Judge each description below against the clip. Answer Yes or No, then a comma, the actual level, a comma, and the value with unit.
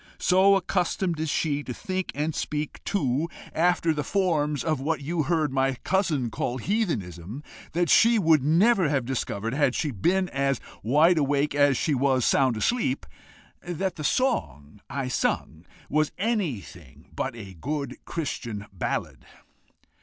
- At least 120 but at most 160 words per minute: Yes, average, 145 wpm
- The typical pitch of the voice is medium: Yes, medium, 150 Hz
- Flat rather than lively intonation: No, average, 5.1 semitones